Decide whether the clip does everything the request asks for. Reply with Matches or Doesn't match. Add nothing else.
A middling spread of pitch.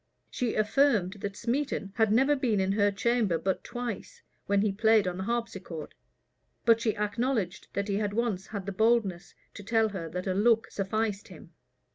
Matches